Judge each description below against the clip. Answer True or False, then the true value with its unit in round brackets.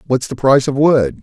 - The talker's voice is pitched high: False (135 Hz)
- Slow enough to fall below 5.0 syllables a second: False (5.6 syllables/s)